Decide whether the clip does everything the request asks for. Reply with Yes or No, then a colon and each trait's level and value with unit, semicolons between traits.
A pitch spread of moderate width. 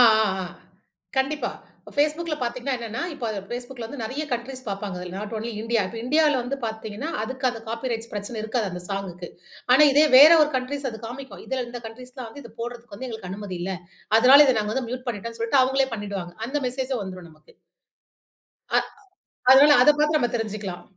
Yes: average, 3.8 semitones